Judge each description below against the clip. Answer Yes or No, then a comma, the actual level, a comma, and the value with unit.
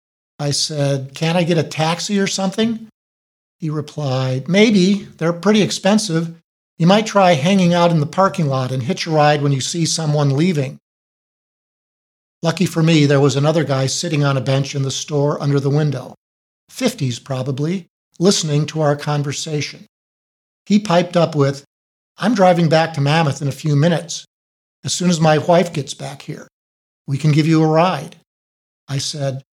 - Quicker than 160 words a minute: Yes, average, 170 wpm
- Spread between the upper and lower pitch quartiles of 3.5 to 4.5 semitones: Yes, average, 3.9 semitones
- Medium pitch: Yes, medium, 155 Hz